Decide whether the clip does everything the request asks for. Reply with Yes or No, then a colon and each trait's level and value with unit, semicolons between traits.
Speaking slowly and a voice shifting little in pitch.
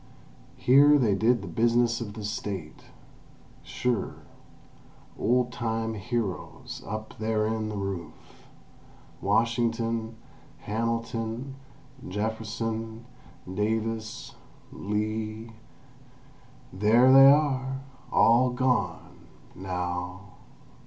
Yes: slow, 70 wpm; narrow, 2.2 semitones